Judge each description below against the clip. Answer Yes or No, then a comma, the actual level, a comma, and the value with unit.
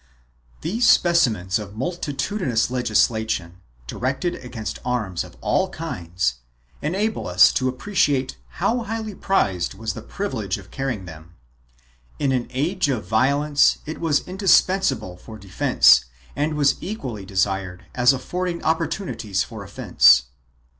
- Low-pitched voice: Yes, low, 130 Hz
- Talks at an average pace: No, slow, 125 wpm